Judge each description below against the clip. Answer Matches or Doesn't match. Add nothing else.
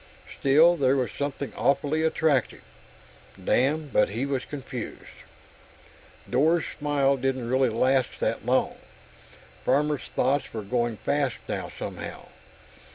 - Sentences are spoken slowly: Matches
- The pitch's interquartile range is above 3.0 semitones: Doesn't match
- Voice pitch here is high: Doesn't match